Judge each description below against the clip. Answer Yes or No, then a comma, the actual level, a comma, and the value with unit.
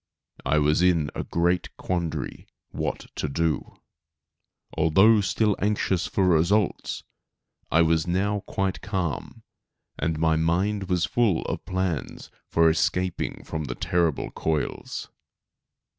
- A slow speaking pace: Yes, slow, 120 wpm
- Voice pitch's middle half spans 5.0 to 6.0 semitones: No, average, 3.1 semitones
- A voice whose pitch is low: Yes, very low, 85 Hz